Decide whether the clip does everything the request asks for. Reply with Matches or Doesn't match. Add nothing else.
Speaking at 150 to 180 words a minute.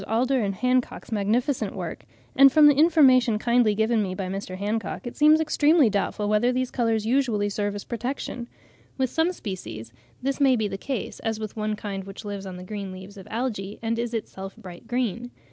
Doesn't match